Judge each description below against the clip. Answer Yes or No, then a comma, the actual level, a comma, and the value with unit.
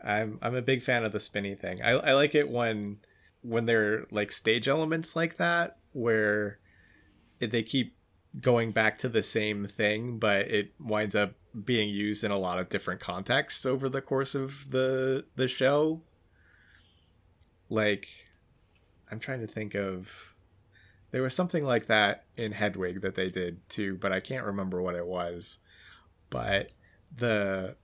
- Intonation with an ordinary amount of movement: Yes, average, 4.2 semitones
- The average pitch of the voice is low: Yes, low, 105 Hz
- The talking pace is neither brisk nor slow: Yes, average, 160 wpm